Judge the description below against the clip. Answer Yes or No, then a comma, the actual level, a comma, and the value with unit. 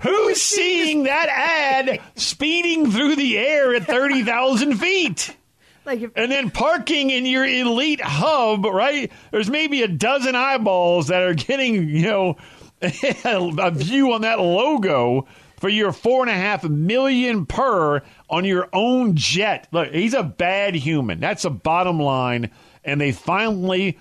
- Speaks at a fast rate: No, average, 145 wpm